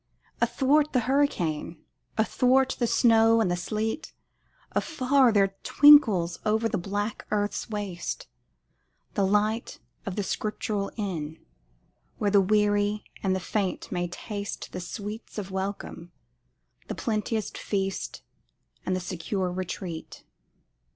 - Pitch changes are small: No, average, 3.2 semitones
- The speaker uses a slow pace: Yes, slow, 120 wpm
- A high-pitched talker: Yes, high, 205 Hz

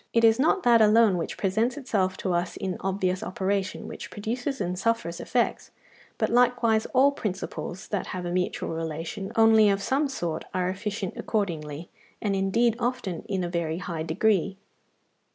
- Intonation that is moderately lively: Yes, average, 4.2 semitones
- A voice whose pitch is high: Yes, high, 195 Hz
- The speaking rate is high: No, average, 165 wpm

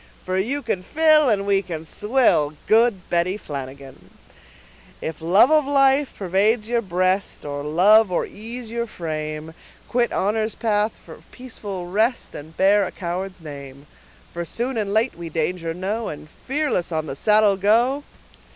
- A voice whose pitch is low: No, high, 195 Hz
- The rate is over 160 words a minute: No, average, 155 wpm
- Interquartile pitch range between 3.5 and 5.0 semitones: No, wide, 5.5 semitones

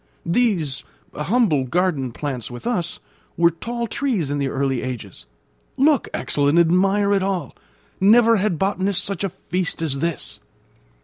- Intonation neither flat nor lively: No, wide, 6.0 semitones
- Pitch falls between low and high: Yes, medium, 175 Hz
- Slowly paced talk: No, average, 145 wpm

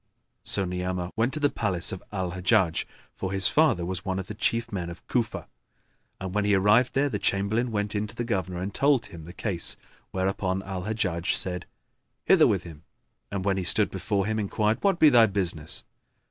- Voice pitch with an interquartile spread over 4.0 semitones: No, average, 3.1 semitones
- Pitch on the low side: Yes, very low, 95 Hz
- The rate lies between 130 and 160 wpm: No, average, 200 wpm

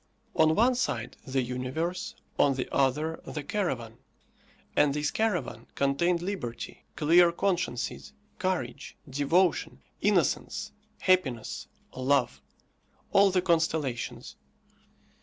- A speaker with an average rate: No, slow, 100 wpm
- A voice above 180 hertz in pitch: No, medium, 155 Hz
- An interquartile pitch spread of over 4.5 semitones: Yes, wide, 5.4 semitones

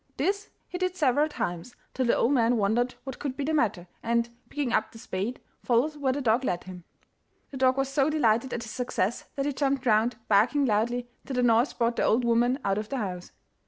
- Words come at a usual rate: No, fast, 225 wpm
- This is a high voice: Yes, high, 245 Hz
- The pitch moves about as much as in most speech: Yes, average, 3.6 semitones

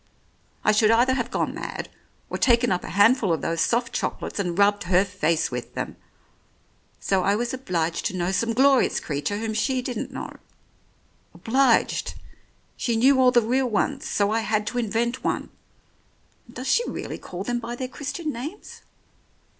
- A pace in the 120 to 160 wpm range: No, average, 175 wpm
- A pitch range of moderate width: Yes, average, 4.4 semitones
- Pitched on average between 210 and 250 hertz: Yes, high, 225 Hz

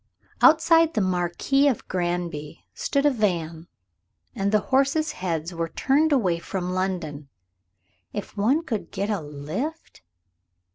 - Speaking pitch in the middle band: No, high, 195 Hz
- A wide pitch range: Yes, wide, 8.3 semitones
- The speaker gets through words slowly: Yes, slow, 130 wpm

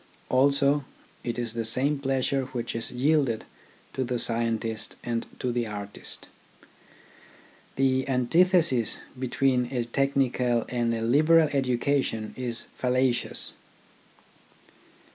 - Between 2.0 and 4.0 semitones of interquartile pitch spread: Yes, average, 2.7 semitones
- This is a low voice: Yes, low, 125 Hz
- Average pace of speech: No, slow, 105 wpm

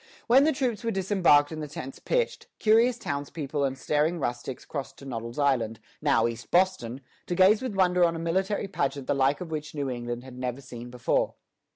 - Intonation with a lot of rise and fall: Yes, wide, 6.4 semitones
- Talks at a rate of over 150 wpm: Yes, average, 200 wpm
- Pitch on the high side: No, medium, 145 Hz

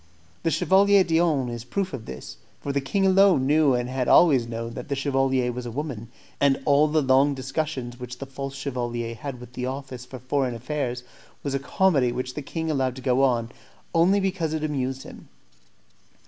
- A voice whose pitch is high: No, low, 135 Hz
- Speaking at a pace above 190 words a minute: Yes, average, 200 wpm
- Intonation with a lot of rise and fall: No, average, 3.3 semitones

